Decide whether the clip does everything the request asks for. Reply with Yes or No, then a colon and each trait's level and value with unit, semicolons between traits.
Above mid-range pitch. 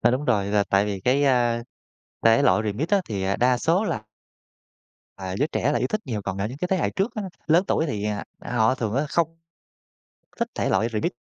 No: low, 120 Hz